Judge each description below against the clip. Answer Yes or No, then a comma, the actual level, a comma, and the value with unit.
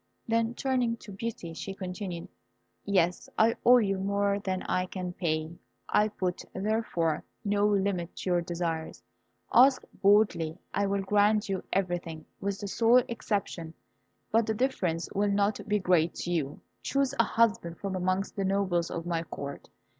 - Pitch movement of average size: Yes, average, 3.3 semitones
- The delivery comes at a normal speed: Yes, average, 160 wpm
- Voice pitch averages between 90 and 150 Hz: No, high, 195 Hz